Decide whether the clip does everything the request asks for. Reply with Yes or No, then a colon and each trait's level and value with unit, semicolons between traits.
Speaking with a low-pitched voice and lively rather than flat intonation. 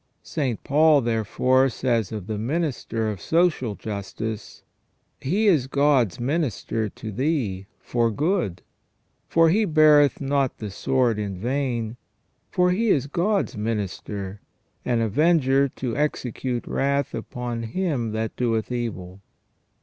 No: low, 125 Hz; average, 5.0 semitones